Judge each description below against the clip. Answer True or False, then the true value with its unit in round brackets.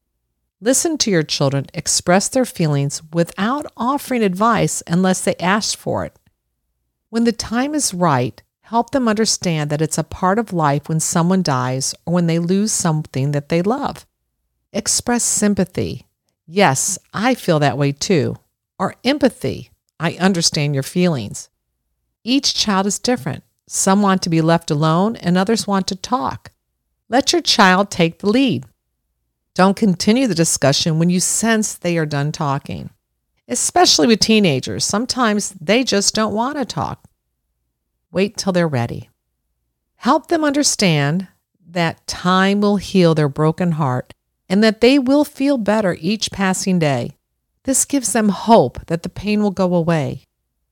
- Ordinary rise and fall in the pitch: False (7.3 semitones)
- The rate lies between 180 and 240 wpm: False (155 wpm)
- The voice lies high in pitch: False (180 Hz)